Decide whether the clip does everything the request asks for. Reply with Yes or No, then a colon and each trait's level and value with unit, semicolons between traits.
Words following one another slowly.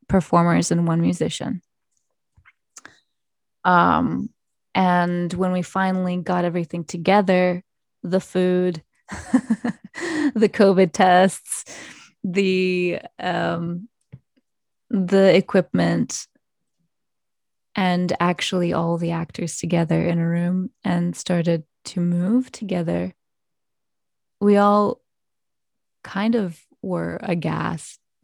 Yes: slow, 85 wpm